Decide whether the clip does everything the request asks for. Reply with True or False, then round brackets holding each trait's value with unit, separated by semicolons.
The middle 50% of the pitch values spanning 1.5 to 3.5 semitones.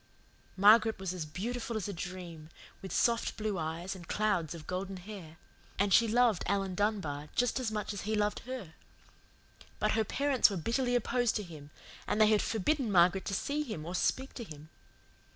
False (4.2 semitones)